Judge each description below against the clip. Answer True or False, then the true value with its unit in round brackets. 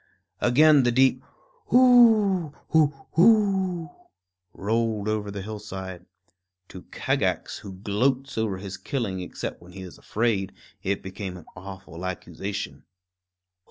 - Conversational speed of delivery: False (120 wpm)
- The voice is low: True (110 Hz)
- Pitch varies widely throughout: True (7.4 semitones)